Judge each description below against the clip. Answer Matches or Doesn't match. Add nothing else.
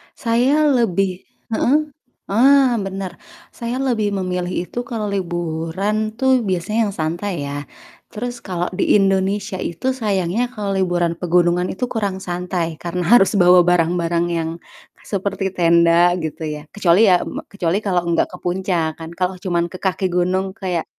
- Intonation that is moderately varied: Matches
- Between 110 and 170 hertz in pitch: Doesn't match